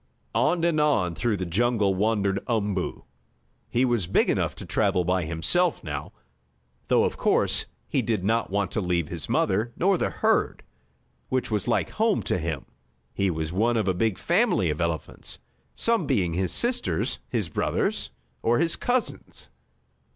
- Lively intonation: Yes, wide, 5.7 semitones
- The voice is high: No, low, 105 Hz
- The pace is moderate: Yes, average, 165 wpm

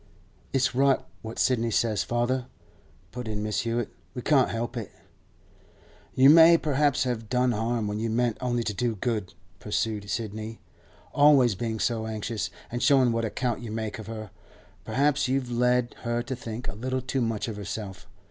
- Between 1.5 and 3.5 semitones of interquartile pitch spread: Yes, narrow, 2.5 semitones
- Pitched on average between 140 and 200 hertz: No, low, 120 Hz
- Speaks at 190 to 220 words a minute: No, average, 175 wpm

